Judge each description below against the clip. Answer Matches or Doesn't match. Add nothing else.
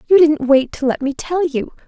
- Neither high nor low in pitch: Doesn't match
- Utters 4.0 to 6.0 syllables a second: Matches